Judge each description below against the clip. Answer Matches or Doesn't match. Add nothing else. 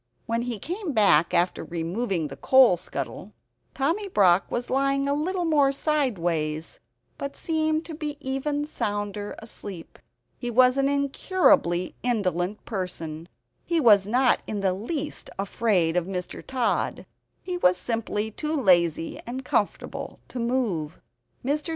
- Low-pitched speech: Doesn't match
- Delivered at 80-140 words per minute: Matches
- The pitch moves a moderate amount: Doesn't match